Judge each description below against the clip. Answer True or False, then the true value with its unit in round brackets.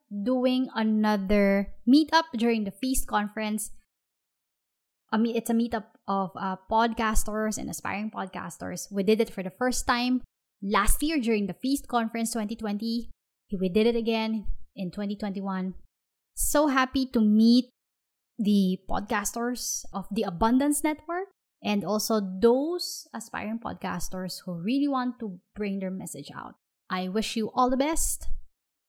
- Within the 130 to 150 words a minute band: True (140 wpm)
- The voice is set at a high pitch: True (220 Hz)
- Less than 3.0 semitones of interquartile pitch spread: False (3.7 semitones)